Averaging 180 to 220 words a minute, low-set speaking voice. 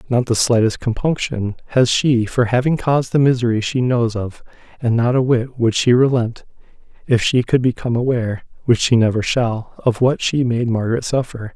Yes: average, 185 wpm; low, 120 Hz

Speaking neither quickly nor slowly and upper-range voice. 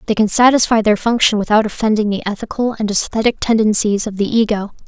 Yes: average, 185 wpm; high, 215 Hz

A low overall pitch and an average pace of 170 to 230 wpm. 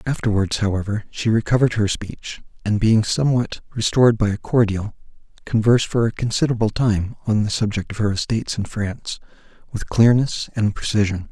No: low, 110 Hz; average, 160 wpm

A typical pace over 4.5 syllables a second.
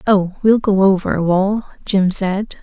No: 3.7 syllables/s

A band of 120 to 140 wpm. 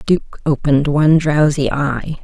Yes: slow, 135 wpm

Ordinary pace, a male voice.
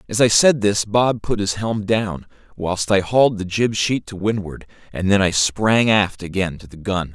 No: fast, 220 wpm; male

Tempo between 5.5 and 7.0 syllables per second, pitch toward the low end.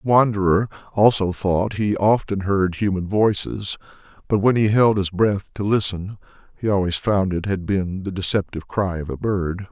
No: 4.8 syllables/s; low, 100 Hz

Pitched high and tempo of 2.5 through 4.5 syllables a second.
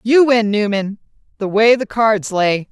Yes: high, 215 Hz; 4.1 syllables/s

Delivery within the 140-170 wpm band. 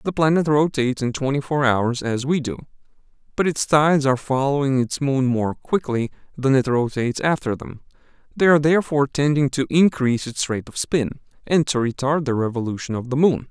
No: average, 185 wpm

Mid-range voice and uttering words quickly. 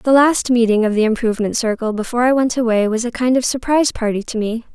No: high, 235 Hz; fast, 240 wpm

